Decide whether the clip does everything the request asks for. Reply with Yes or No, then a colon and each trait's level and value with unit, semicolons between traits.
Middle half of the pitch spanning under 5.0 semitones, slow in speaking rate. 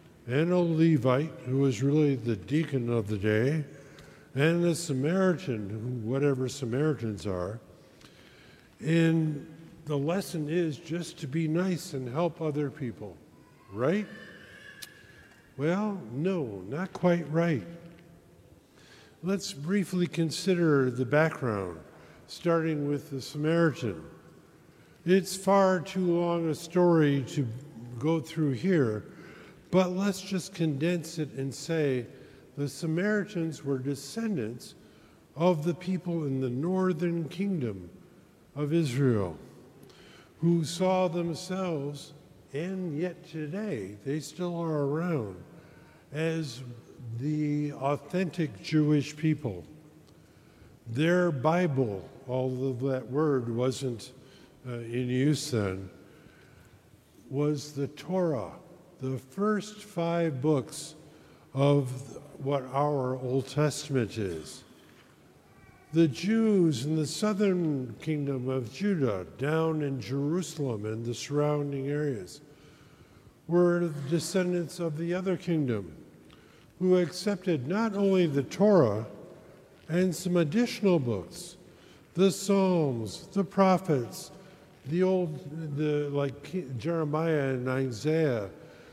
Yes: average, 4.5 semitones; slow, 105 wpm